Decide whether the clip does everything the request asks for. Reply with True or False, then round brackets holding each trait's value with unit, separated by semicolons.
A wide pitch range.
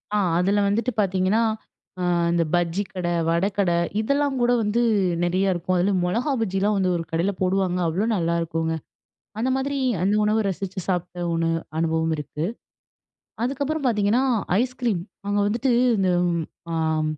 False (4.2 semitones)